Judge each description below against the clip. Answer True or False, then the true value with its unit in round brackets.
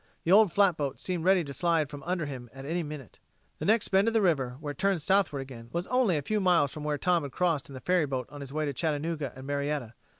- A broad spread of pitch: False (4.4 semitones)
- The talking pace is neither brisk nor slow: False (260 wpm)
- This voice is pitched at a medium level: True (155 Hz)